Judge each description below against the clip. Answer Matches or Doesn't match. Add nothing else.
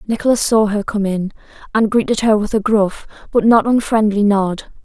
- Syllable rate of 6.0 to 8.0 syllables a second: Doesn't match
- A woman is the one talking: Matches